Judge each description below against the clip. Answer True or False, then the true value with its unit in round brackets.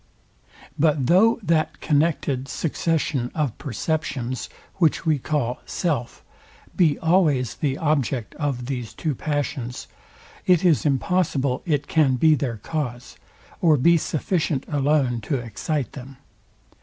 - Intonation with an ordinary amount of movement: True (3.8 semitones)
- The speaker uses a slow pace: True (120 wpm)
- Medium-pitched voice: True (145 Hz)